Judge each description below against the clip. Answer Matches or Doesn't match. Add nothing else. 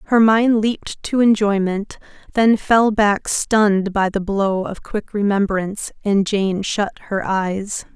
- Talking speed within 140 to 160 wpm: Matches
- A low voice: Doesn't match